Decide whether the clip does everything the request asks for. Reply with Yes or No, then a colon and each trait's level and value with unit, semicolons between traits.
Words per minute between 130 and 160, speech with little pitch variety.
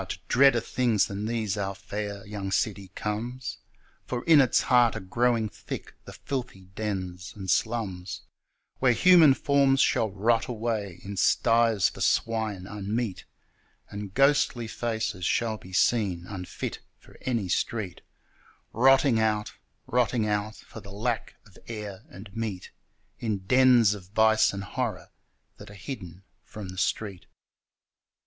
No: average, 140 wpm; average, 3.2 semitones